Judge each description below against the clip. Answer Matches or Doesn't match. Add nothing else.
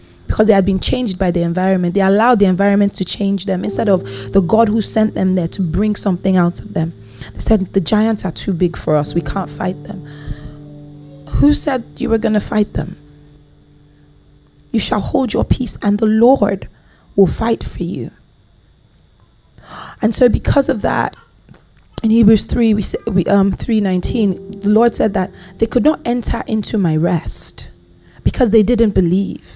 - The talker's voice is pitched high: Matches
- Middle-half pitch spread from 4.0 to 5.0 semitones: Matches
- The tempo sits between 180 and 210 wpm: Matches